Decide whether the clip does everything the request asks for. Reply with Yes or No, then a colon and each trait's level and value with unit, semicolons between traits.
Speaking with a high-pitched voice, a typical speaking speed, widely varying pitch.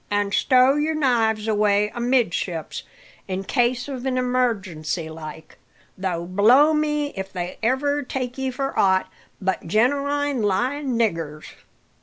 No: high, 235 Hz; slow, 125 wpm; wide, 5.8 semitones